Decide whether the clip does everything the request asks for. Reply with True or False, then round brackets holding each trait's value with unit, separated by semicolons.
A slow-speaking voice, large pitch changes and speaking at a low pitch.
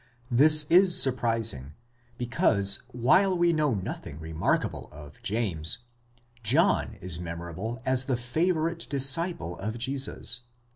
True (110 wpm; 8.2 semitones; 120 Hz)